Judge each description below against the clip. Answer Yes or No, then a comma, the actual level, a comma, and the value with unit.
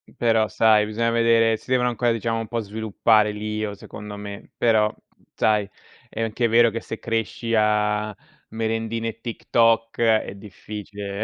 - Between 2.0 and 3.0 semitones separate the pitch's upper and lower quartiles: No, narrow, 1.4 semitones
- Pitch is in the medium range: No, low, 110 Hz